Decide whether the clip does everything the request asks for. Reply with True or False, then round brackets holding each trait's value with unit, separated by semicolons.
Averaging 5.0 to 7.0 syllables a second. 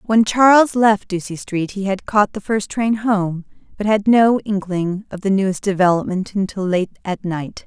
False (4.5 syllables/s)